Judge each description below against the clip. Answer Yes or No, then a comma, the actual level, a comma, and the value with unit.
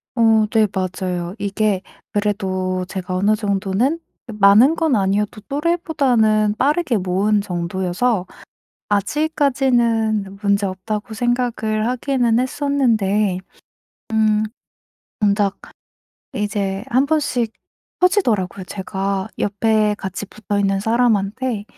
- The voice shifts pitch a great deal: No, average, 3.6 semitones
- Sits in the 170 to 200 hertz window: No, high, 210 Hz